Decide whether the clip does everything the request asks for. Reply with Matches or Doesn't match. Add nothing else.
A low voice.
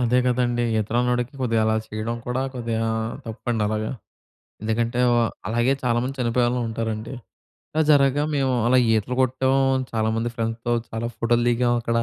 Matches